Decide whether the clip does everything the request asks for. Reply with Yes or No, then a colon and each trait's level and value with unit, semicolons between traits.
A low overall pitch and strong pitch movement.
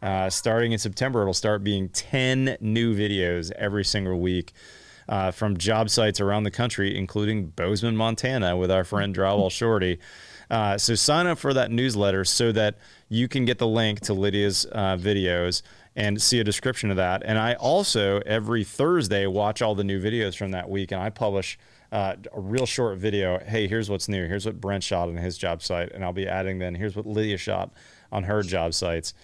No: low, 105 Hz; average, 2.8 semitones